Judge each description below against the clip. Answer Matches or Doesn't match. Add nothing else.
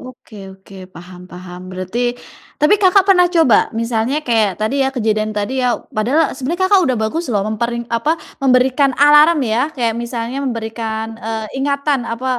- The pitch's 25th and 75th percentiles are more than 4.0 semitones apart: Matches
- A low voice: Doesn't match